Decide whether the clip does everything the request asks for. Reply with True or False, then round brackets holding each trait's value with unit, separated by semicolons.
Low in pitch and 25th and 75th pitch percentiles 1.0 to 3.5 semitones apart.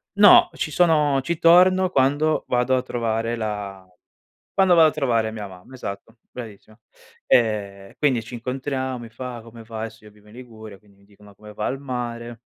False (120 Hz; 3.9 semitones)